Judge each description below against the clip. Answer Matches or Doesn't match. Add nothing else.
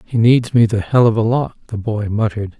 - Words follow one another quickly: Matches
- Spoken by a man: Matches